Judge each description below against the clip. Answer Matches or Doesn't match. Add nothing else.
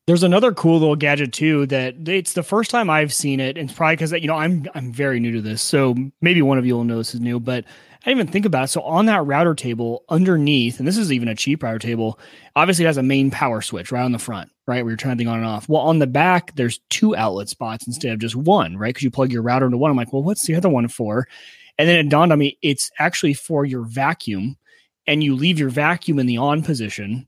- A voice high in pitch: Doesn't match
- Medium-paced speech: Doesn't match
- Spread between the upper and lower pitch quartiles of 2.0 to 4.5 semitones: Doesn't match